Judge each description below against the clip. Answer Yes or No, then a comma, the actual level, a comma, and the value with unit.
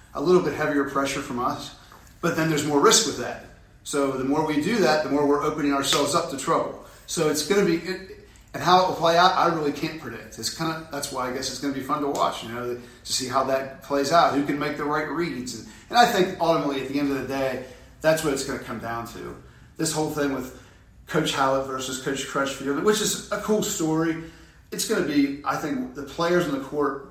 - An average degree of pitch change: Yes, average, 3.5 semitones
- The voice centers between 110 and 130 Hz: No, medium, 140 Hz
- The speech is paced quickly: Yes, fast, 250 wpm